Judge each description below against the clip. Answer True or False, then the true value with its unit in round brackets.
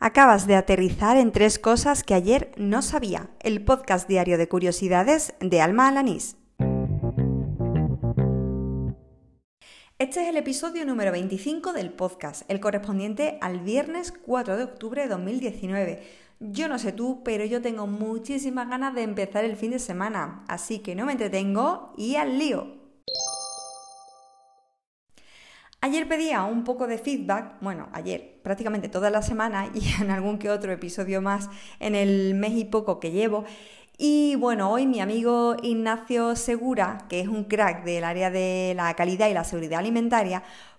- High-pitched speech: True (210 Hz)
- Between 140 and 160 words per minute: True (155 wpm)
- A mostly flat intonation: False (5.2 semitones)